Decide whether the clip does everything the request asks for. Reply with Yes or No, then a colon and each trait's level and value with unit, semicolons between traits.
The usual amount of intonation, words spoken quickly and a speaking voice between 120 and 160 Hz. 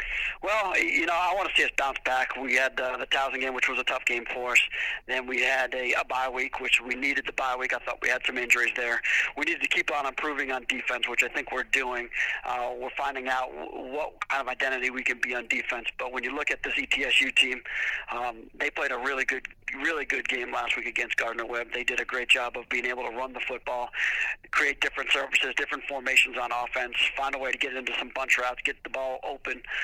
No: narrow, 1.0 semitones; fast, 245 wpm; low, 130 Hz